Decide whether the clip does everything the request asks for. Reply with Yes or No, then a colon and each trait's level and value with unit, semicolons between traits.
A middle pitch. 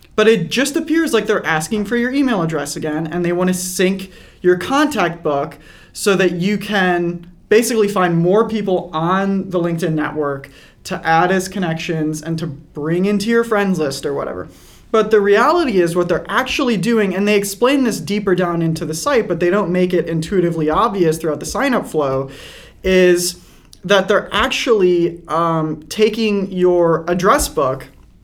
Yes: medium, 180 Hz